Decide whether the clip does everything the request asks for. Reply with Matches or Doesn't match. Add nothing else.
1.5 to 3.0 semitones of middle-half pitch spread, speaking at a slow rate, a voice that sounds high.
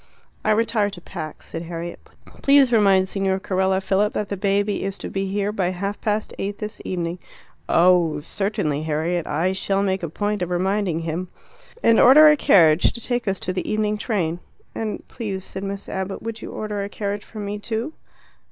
Doesn't match